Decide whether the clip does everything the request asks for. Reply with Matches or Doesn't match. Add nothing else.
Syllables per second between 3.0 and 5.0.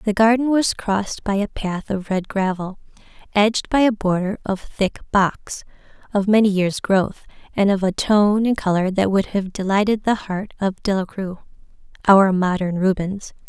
Matches